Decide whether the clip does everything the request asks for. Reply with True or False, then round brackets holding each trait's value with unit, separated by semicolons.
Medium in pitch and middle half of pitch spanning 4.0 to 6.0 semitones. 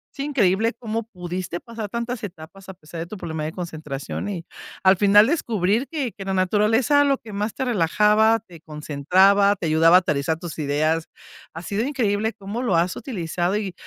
False (195 Hz; 4.9 semitones)